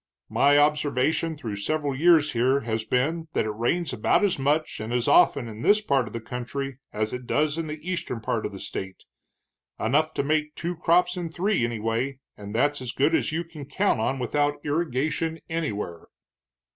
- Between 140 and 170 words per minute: No, average, 190 wpm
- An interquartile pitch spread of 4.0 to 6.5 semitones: Yes, average, 5.1 semitones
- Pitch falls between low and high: Yes, medium, 145 Hz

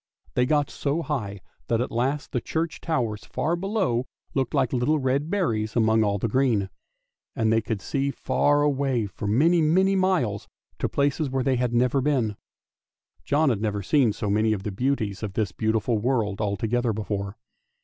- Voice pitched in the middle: No, low, 125 Hz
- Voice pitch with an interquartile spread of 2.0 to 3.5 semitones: No, average, 4.9 semitones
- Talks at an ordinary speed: Yes, average, 180 wpm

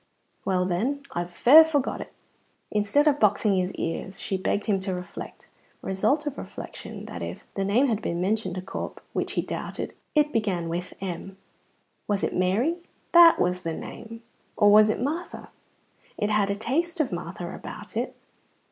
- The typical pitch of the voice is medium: No, high, 205 Hz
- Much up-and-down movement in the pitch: Yes, wide, 6.5 semitones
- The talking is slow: No, average, 175 wpm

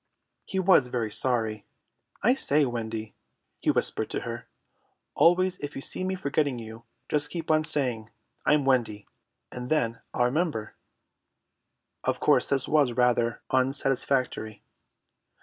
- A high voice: No, low, 130 Hz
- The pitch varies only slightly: No, average, 4.7 semitones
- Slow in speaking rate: Yes, slow, 130 wpm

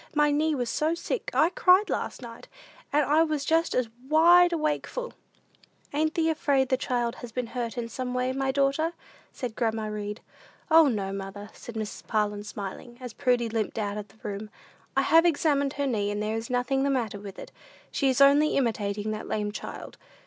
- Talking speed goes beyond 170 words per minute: Yes, average, 195 wpm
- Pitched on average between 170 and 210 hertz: No, very high, 250 Hz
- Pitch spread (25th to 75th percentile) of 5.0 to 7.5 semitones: Yes, wide, 5.5 semitones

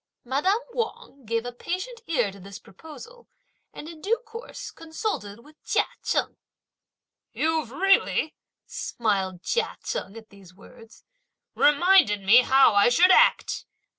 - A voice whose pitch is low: No, very high, 275 Hz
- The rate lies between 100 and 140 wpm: Yes, slow, 135 wpm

